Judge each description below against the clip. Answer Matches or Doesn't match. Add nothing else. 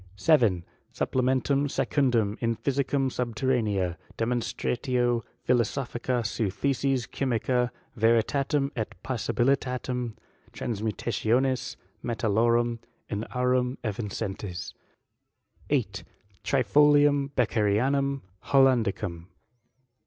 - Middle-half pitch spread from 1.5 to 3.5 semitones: Matches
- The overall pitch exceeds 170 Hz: Doesn't match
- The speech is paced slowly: Matches